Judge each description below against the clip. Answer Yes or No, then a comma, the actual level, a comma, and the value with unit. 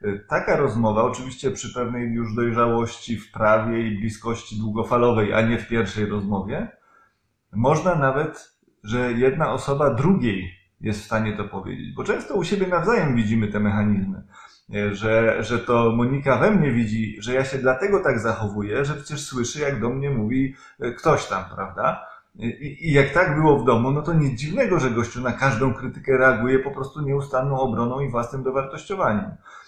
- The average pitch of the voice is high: No, low, 120 Hz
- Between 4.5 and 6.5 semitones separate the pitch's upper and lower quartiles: No, average, 3.6 semitones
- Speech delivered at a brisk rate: Yes, fast, 170 wpm